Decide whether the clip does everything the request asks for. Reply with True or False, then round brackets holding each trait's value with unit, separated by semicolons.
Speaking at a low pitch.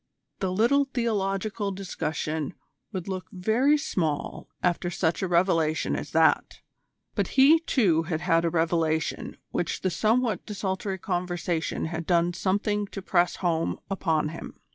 False (185 Hz)